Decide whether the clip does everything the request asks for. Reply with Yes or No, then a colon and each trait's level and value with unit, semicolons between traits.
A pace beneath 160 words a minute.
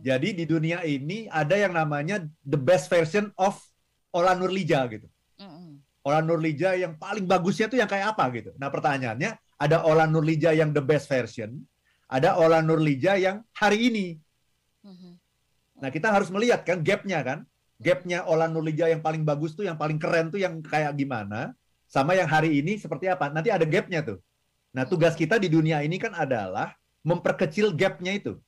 No: fast, 170 wpm